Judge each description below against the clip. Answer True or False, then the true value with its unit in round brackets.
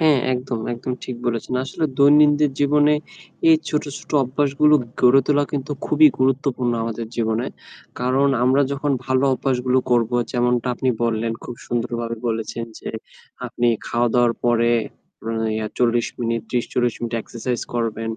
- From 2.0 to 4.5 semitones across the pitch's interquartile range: True (2.8 semitones)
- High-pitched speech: False (125 Hz)